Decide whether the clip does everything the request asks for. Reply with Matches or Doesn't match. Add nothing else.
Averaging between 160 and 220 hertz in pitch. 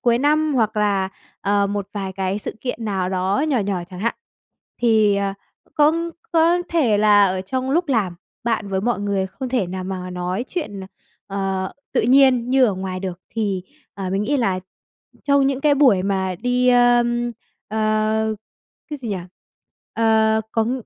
Matches